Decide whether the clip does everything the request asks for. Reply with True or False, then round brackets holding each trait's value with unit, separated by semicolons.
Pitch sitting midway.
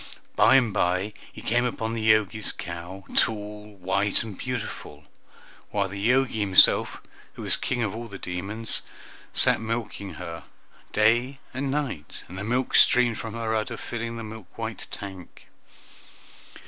False (110 Hz)